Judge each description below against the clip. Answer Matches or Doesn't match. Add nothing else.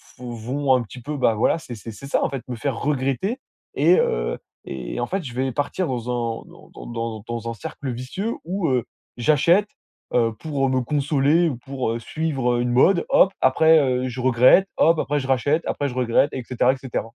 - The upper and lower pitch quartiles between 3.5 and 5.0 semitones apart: Matches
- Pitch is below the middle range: Matches